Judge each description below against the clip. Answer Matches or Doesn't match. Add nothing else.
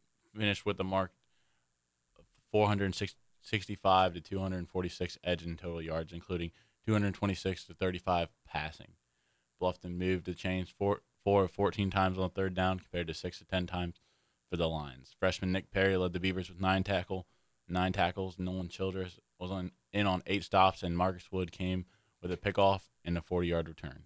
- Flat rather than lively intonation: Matches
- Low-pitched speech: Matches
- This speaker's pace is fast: Doesn't match